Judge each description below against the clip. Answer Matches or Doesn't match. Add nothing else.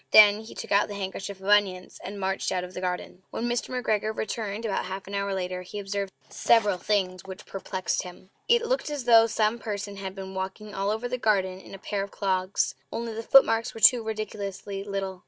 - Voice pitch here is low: Doesn't match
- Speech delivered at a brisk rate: Matches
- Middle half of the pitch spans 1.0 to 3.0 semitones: Matches